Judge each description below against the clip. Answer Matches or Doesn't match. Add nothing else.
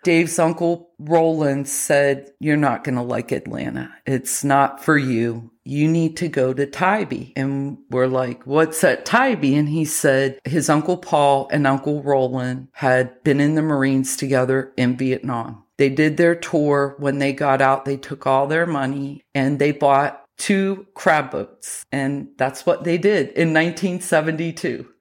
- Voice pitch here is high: Doesn't match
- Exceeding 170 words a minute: Doesn't match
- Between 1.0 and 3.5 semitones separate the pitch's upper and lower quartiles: Matches